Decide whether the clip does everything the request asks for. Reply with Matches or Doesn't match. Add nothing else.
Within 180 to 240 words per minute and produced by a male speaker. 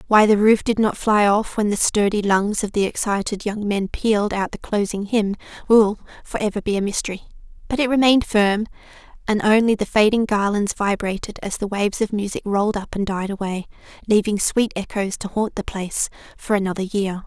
Doesn't match